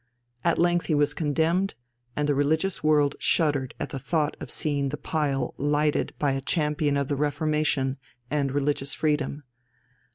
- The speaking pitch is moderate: Yes, medium, 150 Hz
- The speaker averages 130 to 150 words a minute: No, average, 160 wpm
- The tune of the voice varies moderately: No, narrow, 1.6 semitones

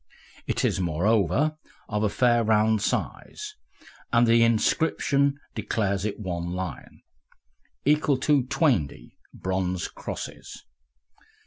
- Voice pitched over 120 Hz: No, low, 110 Hz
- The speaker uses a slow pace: Yes, slow, 105 wpm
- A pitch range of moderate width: No, wide, 6.0 semitones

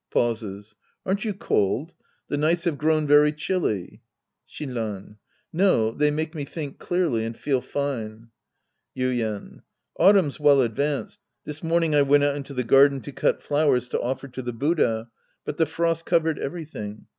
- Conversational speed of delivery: Yes, average, 155 wpm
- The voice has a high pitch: No, medium, 145 Hz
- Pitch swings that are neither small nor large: Yes, average, 4.8 semitones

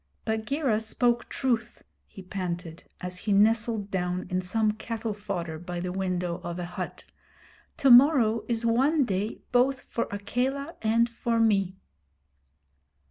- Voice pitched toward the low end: No, high, 215 Hz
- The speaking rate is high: No, slow, 135 wpm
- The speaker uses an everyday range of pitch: Yes, average, 4.5 semitones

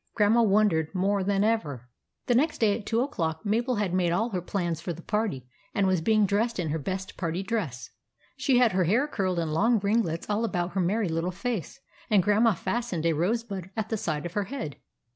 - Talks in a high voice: Yes, high, 200 Hz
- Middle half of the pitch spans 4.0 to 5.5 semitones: Yes, average, 4.6 semitones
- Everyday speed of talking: No, fast, 220 wpm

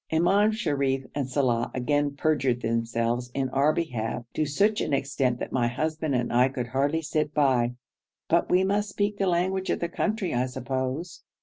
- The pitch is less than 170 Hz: Yes, medium, 140 Hz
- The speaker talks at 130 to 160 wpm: No, average, 180 wpm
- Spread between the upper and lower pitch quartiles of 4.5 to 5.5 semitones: Yes, average, 5.2 semitones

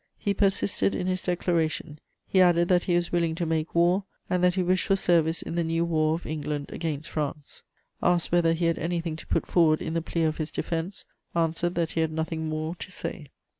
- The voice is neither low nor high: Yes, medium, 165 Hz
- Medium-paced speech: No, fast, 220 wpm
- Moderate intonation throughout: No, narrow, 1.7 semitones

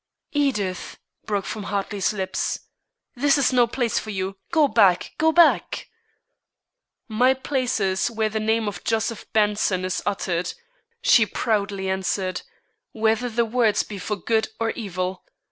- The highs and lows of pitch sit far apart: No, average, 3.6 semitones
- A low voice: No, high, 215 Hz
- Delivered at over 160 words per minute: No, average, 145 wpm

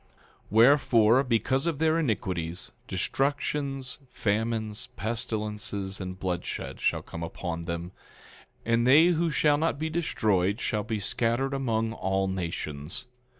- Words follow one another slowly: Yes, slow, 125 wpm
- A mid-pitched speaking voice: No, low, 115 Hz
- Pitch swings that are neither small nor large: No, wide, 6.1 semitones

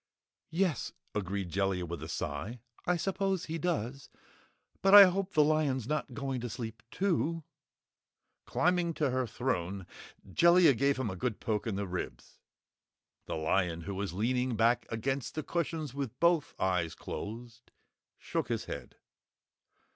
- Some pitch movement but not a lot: No, wide, 8.0 semitones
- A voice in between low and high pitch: No, low, 125 Hz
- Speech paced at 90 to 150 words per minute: Yes, average, 145 wpm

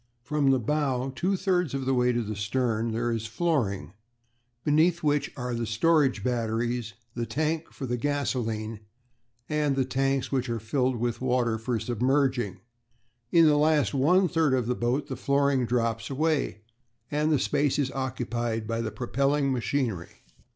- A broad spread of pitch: No, average, 3.8 semitones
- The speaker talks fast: No, average, 165 wpm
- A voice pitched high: No, low, 130 Hz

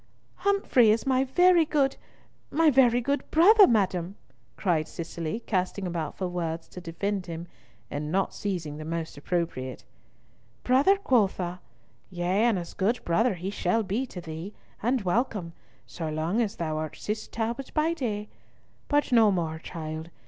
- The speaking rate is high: No, average, 150 wpm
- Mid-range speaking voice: No, high, 195 Hz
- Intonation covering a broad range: Yes, wide, 6.6 semitones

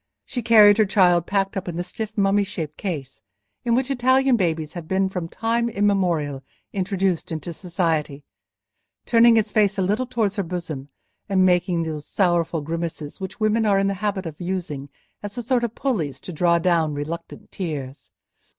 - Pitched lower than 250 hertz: Yes, medium, 185 Hz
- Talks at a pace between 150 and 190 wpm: Yes, average, 180 wpm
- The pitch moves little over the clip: No, average, 4.3 semitones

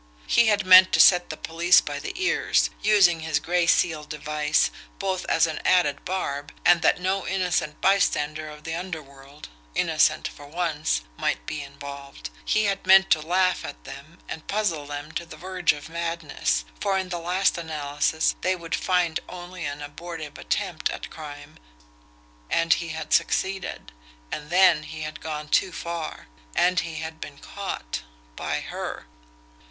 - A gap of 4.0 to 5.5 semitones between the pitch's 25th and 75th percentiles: No, average, 3.3 semitones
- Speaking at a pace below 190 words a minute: Yes, average, 165 wpm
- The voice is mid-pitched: Yes, medium, 165 Hz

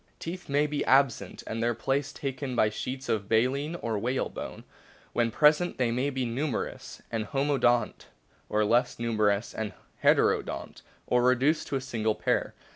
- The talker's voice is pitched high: No, low, 125 Hz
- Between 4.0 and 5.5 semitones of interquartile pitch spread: No, average, 3.5 semitones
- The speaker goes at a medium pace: Yes, average, 165 wpm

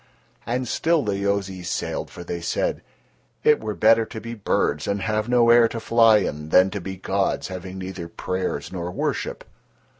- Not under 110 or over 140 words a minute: No, average, 180 wpm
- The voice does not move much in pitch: No, average, 3.6 semitones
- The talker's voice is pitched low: Yes, low, 100 Hz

